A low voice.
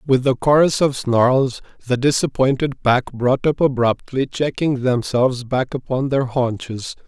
Yes: low, 130 Hz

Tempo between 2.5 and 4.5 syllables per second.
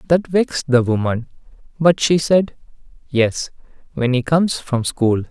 Yes: 4.4 syllables/s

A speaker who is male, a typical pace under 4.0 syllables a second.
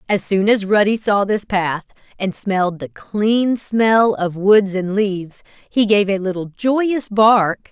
No: female; 3.7 syllables/s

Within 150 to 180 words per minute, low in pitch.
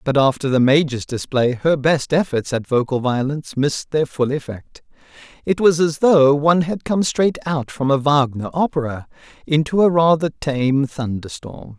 No: average, 170 wpm; medium, 145 Hz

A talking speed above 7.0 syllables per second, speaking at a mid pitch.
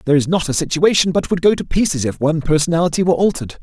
Yes: 7.8 syllables/s; medium, 160 Hz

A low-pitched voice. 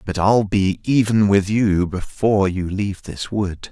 Yes: low, 100 Hz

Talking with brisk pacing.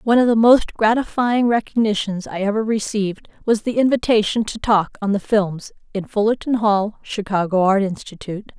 No: average, 160 wpm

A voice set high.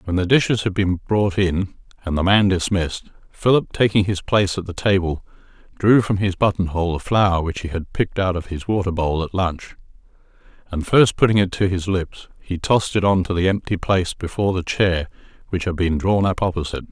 No: very low, 95 Hz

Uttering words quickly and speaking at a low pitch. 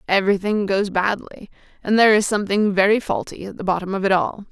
No: fast, 215 wpm; high, 200 Hz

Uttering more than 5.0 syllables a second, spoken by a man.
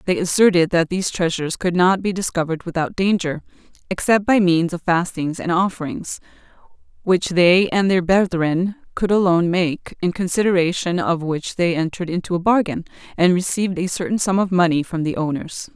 No: 5.5 syllables/s; female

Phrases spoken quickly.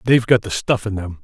Yes: fast, 290 wpm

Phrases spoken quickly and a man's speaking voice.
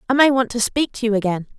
No: fast, 305 wpm; female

